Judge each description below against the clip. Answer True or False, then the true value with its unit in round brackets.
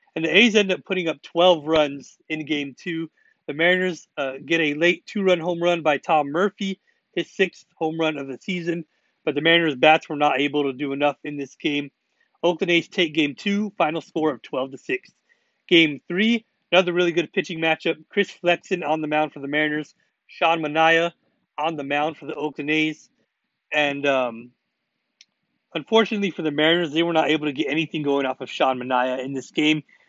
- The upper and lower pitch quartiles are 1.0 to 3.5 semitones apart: True (2.9 semitones)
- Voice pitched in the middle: True (160 Hz)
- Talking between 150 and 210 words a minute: True (200 wpm)